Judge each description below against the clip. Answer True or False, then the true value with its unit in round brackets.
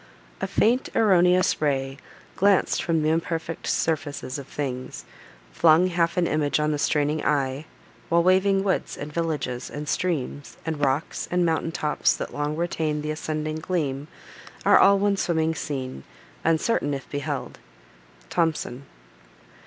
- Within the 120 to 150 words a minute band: True (140 wpm)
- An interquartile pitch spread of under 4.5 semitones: True (2.9 semitones)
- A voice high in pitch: False (155 Hz)